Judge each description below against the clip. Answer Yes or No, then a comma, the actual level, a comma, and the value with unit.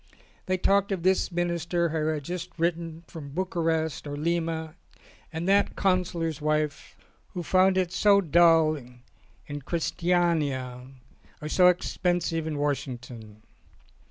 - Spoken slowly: Yes, slow, 125 wpm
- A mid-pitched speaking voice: Yes, medium, 165 Hz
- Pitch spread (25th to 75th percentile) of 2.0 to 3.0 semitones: Yes, average, 2.7 semitones